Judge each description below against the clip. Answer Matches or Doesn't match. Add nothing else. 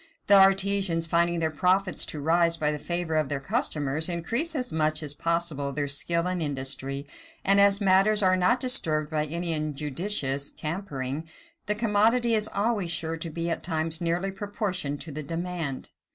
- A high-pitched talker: Doesn't match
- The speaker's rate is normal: Matches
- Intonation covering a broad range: Doesn't match